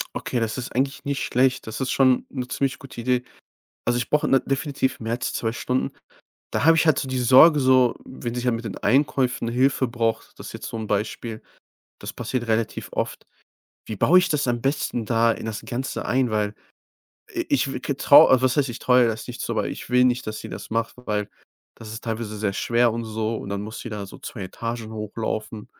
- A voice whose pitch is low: Yes, low, 120 Hz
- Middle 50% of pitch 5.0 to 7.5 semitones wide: No, narrow, 2.6 semitones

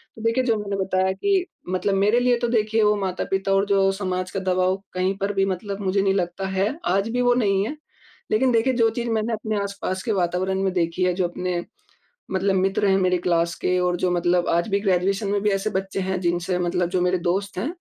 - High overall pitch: Yes, high, 195 Hz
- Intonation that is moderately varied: No, narrow, 2.3 semitones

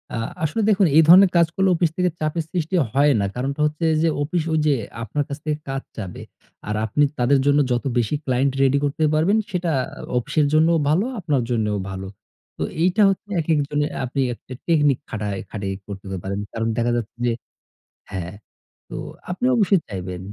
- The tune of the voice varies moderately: No, wide, 6.4 semitones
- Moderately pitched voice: Yes, medium, 145 Hz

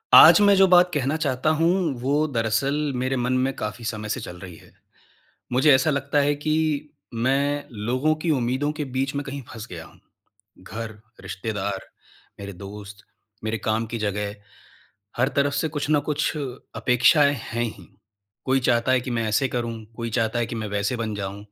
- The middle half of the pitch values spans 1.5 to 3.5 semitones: No, average, 4.6 semitones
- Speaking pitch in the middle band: No, low, 125 Hz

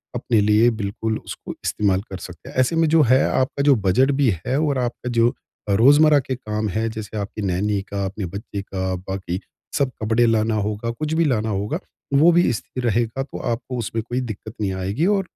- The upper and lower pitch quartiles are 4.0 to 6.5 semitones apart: Yes, average, 4.4 semitones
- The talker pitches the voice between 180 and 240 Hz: No, low, 110 Hz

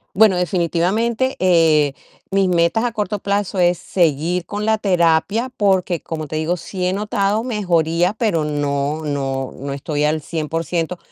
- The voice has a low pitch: No, medium, 175 Hz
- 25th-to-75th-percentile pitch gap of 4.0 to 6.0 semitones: Yes, average, 4.4 semitones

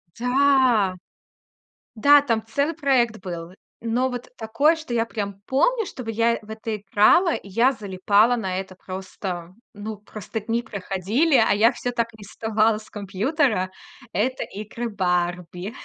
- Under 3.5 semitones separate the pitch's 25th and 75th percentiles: No, average, 4.0 semitones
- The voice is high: Yes, high, 220 Hz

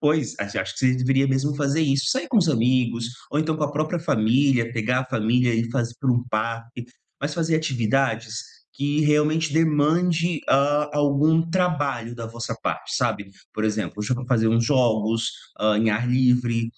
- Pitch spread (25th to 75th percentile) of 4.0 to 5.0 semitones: Yes, average, 4.4 semitones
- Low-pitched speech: Yes, low, 130 Hz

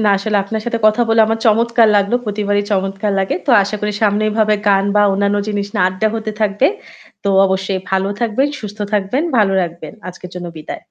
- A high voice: Yes, high, 205 Hz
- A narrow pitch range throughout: Yes, narrow, 2.0 semitones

